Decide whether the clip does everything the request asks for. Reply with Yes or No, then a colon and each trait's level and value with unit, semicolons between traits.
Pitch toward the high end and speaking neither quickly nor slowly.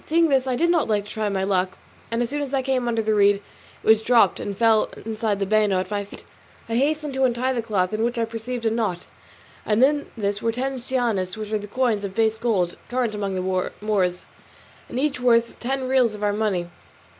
No: high, 225 Hz; fast, 235 wpm